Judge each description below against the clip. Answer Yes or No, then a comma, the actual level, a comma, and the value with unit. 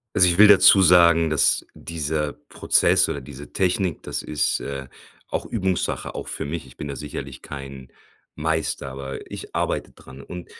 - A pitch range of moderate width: Yes, average, 4.1 semitones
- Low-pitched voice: Yes, very low, 75 Hz